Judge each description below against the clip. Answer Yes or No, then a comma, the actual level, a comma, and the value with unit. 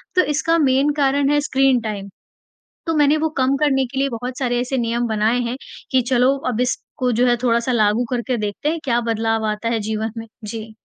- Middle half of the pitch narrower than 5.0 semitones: Yes, average, 3.0 semitones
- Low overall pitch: No, high, 245 Hz